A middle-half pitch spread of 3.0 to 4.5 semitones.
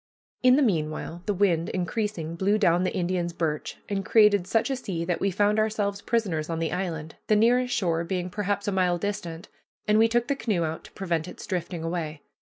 Yes: average, 3.9 semitones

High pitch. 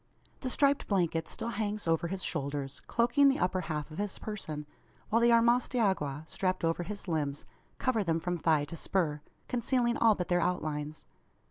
No: medium, 180 Hz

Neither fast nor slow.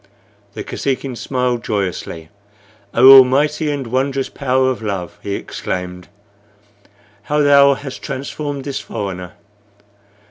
No: slow, 110 wpm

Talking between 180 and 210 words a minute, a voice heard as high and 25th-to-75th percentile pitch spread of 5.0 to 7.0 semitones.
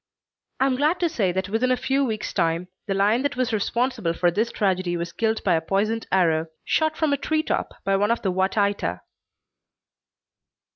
Yes: average, 200 wpm; high, 205 Hz; wide, 5.6 semitones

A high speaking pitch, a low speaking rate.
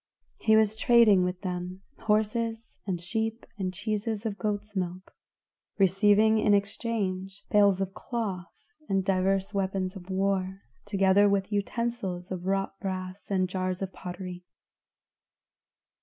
Yes: high, 195 Hz; slow, 125 wpm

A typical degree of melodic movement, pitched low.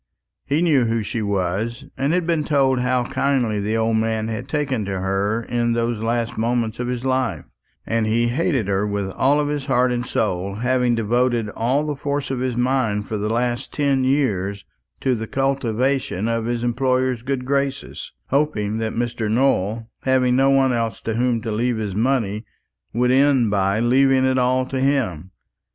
Yes: average, 3.1 semitones; low, 120 Hz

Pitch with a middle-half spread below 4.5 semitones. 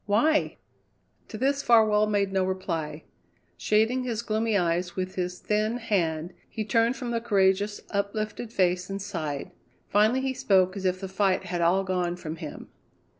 Yes: average, 3.3 semitones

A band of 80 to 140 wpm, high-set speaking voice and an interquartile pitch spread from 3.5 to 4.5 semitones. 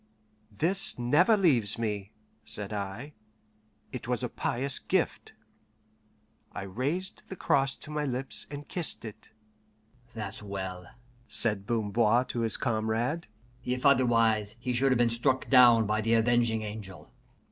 No: slow, 135 wpm; low, 120 Hz; average, 3.8 semitones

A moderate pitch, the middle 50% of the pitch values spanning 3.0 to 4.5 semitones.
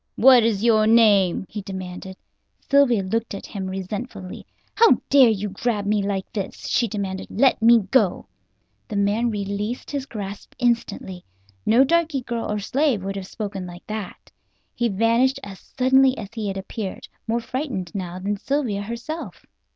No: high, 215 Hz; average, 3.7 semitones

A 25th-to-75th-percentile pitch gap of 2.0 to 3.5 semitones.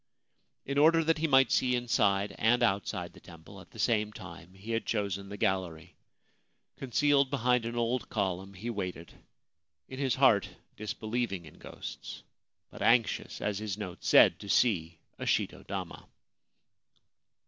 No: average, 4.3 semitones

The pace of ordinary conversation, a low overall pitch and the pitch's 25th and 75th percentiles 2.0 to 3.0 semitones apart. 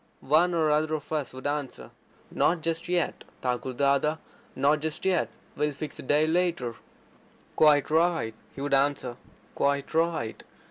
No: average, 150 wpm; medium, 150 Hz; average, 2.7 semitones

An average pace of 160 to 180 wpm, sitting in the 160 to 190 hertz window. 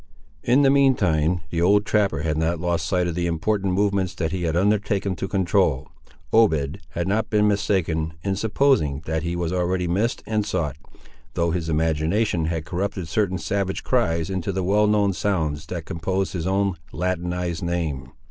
No: average, 175 wpm; very low, 90 Hz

